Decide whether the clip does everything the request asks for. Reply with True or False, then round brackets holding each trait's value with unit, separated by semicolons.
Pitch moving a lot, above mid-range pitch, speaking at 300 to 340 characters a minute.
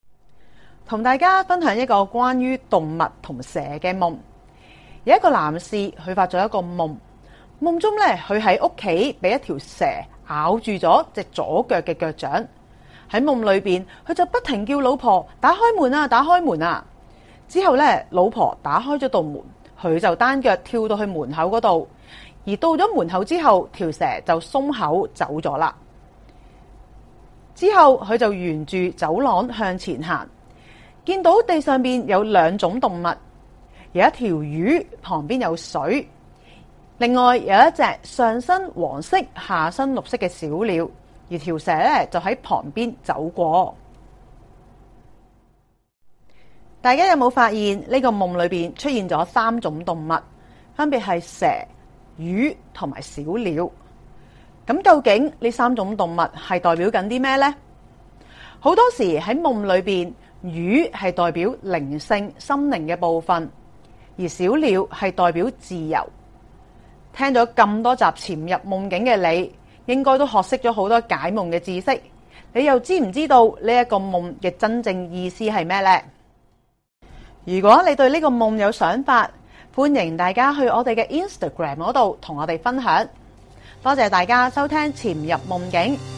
False (6.9 semitones; 210 Hz; 215 characters per minute)